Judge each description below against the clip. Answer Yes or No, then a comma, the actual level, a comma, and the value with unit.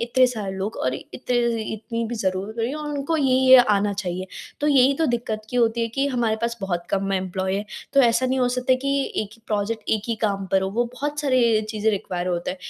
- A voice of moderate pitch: No, high, 225 Hz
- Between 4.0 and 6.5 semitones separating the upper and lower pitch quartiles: Yes, average, 4.5 semitones